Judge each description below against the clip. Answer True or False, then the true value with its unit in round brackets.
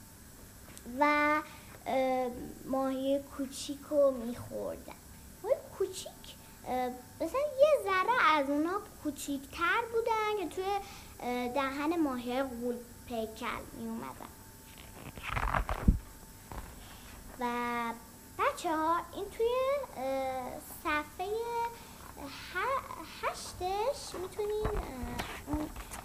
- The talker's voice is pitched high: True (295 Hz)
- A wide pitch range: True (6.6 semitones)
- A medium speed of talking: False (65 wpm)